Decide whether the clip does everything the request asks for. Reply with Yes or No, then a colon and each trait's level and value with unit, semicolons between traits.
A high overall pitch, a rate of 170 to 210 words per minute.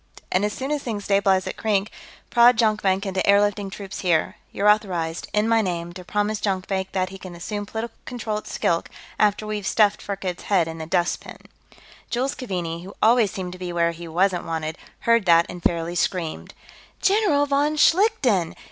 Yes: high, 195 Hz; average, 185 wpm